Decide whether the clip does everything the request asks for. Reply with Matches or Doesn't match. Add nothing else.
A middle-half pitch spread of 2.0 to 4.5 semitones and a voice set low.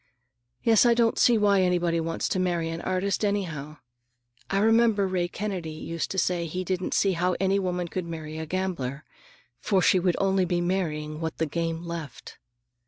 Doesn't match